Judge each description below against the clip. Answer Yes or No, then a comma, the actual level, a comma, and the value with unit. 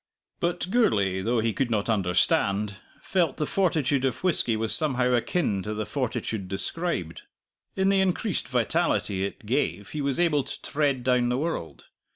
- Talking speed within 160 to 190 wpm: Yes, average, 165 wpm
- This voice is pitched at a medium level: No, low, 125 Hz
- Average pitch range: No, wide, 7.3 semitones